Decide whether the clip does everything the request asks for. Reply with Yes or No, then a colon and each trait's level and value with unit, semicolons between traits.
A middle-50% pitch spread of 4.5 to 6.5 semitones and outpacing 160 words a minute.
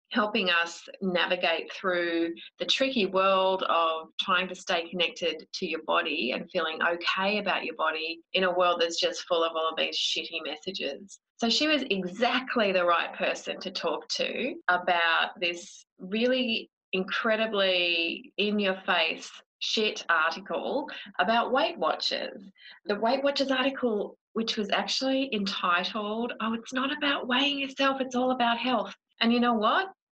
No: wide, 5.4 semitones; average, 155 wpm